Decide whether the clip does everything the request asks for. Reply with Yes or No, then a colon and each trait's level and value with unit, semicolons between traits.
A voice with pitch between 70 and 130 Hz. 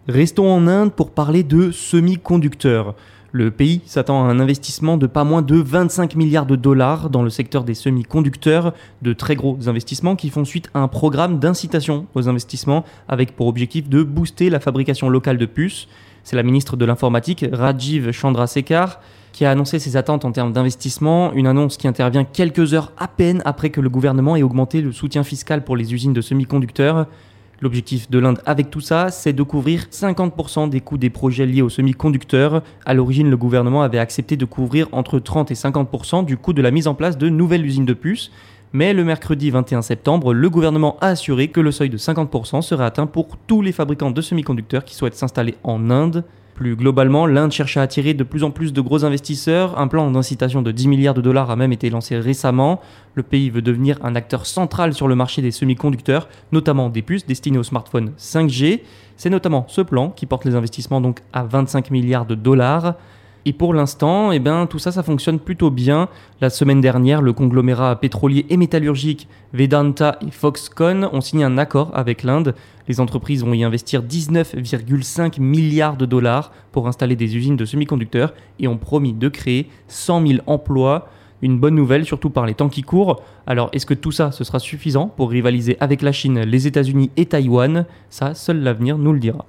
No: medium, 140 Hz